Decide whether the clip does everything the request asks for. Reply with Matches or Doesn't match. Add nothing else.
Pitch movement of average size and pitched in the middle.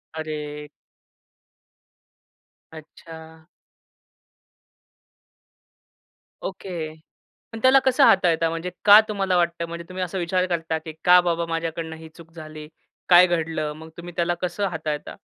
Doesn't match